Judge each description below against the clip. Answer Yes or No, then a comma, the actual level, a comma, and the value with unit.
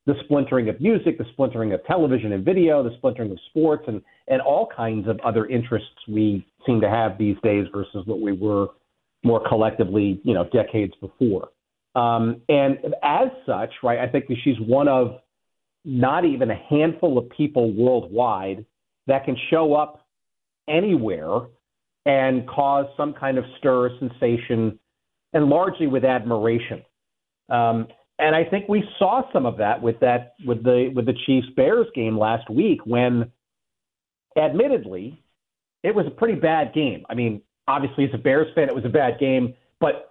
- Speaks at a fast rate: No, average, 170 wpm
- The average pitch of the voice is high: No, low, 125 Hz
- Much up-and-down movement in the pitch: No, average, 4.0 semitones